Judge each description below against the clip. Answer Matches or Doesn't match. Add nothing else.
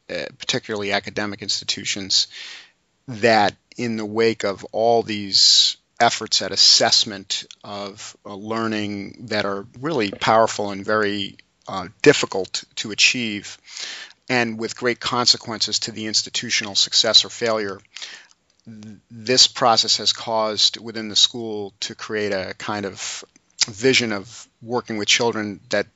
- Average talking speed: Doesn't match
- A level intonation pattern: Matches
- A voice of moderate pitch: Doesn't match